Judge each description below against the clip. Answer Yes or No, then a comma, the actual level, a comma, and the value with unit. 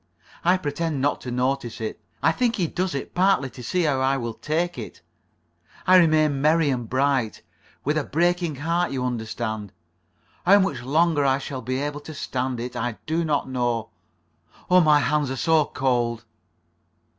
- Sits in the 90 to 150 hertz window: Yes, medium, 140 Hz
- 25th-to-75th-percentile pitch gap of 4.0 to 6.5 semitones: Yes, average, 4.5 semitones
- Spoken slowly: No, average, 175 wpm